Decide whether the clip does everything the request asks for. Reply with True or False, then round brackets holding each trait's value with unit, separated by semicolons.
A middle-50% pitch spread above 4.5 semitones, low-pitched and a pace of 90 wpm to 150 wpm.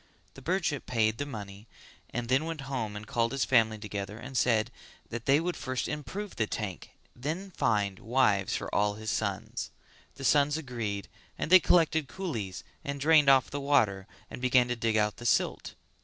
False (4.9 semitones; 120 Hz; 185 wpm)